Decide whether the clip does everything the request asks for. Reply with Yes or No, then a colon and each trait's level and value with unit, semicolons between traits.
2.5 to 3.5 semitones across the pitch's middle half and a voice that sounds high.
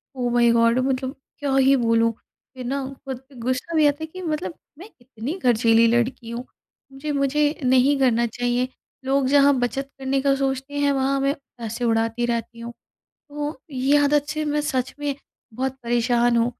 Yes: average, 2.8 semitones; very high, 260 Hz